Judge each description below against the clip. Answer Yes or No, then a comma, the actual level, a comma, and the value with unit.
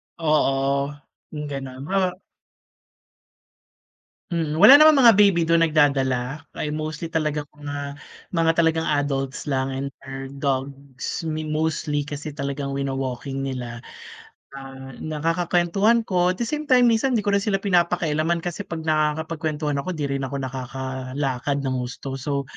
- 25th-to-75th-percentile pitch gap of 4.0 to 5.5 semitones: No, average, 3.5 semitones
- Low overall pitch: No, medium, 150 Hz